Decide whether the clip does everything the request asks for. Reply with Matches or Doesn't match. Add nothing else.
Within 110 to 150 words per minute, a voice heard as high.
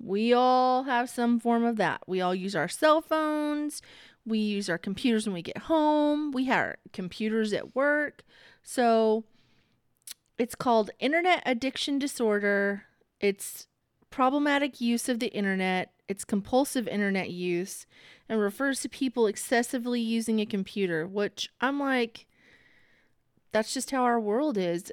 Matches